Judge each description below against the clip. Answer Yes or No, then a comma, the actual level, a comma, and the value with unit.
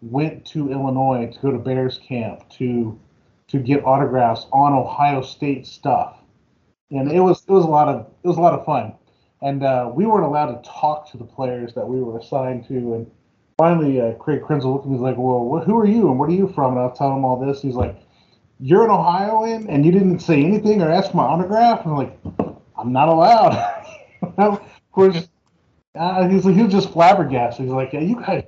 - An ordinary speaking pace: No, fast, 220 wpm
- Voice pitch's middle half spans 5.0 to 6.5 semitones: Yes, wide, 5.4 semitones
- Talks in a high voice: No, medium, 140 Hz